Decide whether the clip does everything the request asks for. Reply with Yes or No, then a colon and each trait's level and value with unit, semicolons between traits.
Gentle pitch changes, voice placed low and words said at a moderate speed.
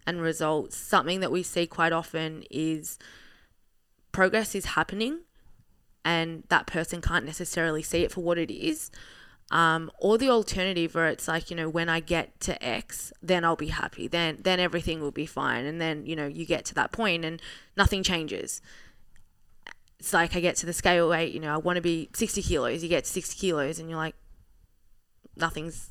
No: narrow, 1.9 semitones; medium, 165 Hz; average, 195 wpm